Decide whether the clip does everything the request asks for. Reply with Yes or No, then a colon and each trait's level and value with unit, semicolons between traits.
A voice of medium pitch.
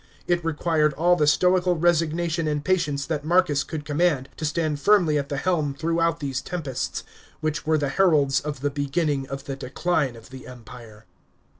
Yes: medium, 150 Hz